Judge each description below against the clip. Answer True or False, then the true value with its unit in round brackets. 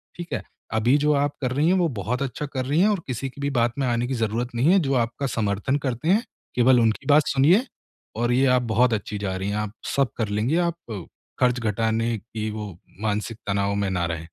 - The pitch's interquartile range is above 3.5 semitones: True (4.6 semitones)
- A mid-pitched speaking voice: False (120 Hz)